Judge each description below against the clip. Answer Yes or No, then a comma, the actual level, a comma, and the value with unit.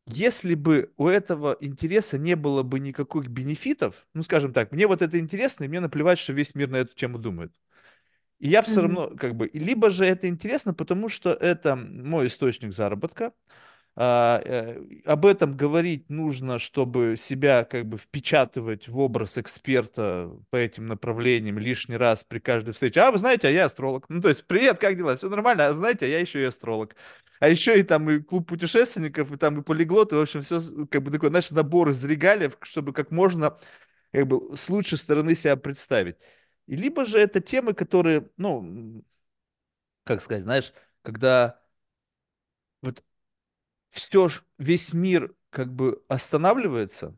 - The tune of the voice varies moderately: No, wide, 5.7 semitones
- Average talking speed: No, fast, 175 wpm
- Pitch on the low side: No, medium, 150 Hz